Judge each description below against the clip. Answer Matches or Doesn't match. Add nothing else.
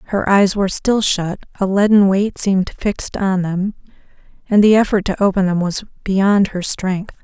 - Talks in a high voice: Matches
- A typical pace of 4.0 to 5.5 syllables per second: Matches